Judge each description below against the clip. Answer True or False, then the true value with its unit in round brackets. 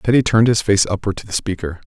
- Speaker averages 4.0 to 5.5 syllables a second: False (6.7 syllables/s)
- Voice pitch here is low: True (105 Hz)